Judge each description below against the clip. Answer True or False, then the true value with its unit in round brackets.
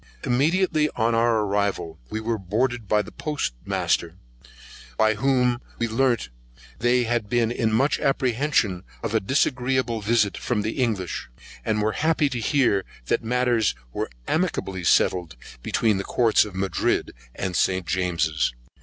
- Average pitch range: True (3.7 semitones)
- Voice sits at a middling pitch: False (115 Hz)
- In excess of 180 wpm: False (145 wpm)